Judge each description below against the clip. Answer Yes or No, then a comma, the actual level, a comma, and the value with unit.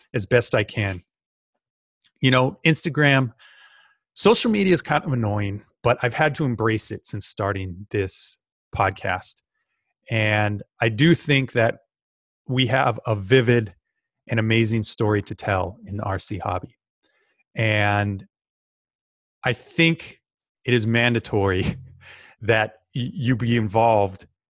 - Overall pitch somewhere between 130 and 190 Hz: No, low, 115 Hz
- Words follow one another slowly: Yes, slow, 125 wpm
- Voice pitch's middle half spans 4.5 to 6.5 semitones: No, average, 4.1 semitones